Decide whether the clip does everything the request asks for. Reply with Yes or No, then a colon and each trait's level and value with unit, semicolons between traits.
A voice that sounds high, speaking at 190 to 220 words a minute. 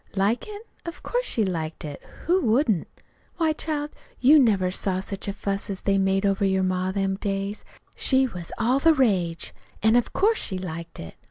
Yes: high, 200 Hz; average, 195 wpm